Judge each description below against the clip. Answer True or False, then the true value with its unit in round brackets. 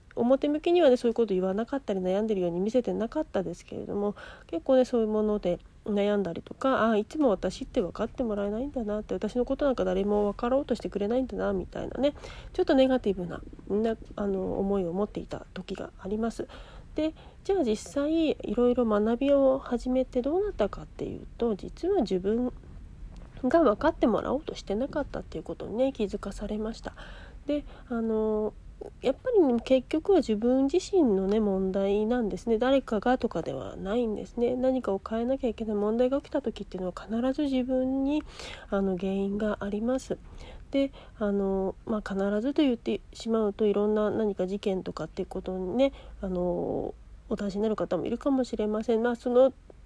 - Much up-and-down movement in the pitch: False (4.4 semitones)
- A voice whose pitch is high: True (225 Hz)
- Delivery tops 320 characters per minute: True (390 characters per minute)